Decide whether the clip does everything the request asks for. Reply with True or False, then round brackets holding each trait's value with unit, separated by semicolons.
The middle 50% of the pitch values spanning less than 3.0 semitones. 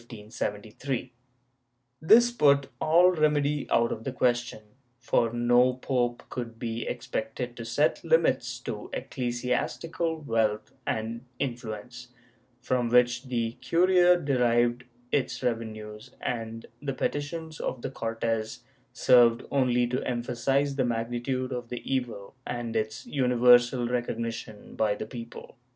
True (2.4 semitones)